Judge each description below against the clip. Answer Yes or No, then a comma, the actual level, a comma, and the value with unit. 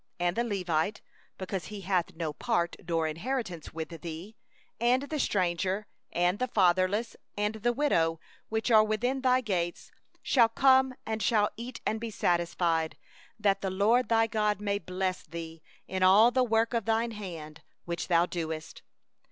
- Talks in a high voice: Yes, high, 200 Hz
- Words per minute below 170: Yes, average, 160 wpm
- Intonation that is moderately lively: Yes, average, 4.7 semitones